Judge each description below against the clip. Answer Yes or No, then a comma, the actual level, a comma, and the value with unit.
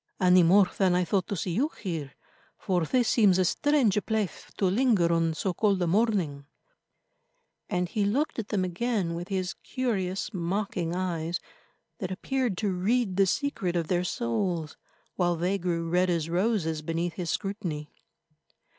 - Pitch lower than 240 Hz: Yes, medium, 185 Hz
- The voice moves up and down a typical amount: Yes, average, 3.3 semitones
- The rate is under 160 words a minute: No, average, 165 wpm